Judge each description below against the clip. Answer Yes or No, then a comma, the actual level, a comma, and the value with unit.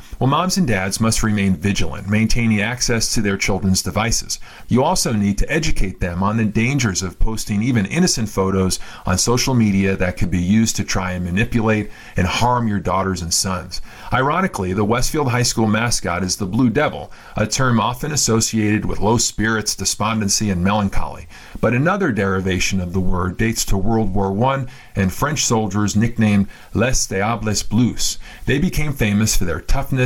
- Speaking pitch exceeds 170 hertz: No, low, 105 Hz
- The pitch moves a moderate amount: Yes, average, 3.4 semitones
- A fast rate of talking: No, average, 175 wpm